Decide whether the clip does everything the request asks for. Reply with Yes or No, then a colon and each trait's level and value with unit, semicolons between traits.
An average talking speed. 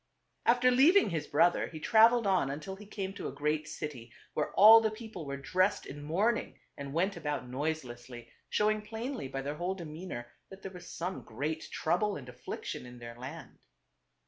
Yes: average, 180 wpm